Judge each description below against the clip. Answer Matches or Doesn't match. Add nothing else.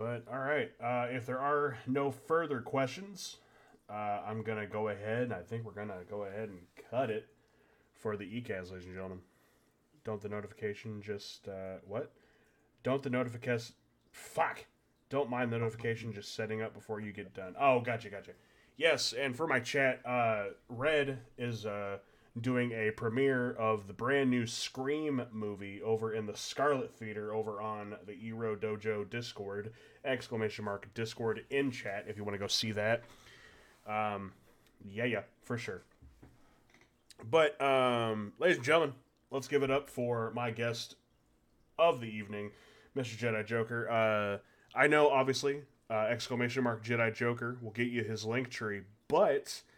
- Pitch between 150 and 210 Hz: Doesn't match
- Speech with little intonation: Doesn't match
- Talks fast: Doesn't match